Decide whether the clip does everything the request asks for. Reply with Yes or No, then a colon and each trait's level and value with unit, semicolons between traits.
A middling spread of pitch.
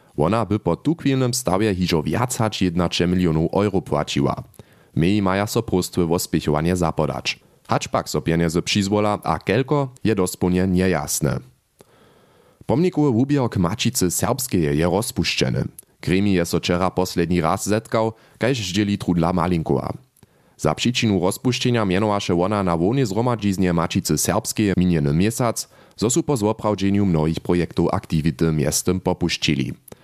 Yes: average, 4.4 semitones